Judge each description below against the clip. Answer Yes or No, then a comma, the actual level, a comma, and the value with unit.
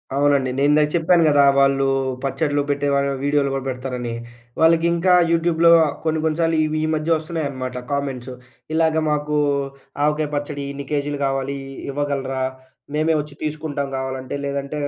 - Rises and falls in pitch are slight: Yes, narrow, 2.2 semitones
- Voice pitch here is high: No, medium, 145 Hz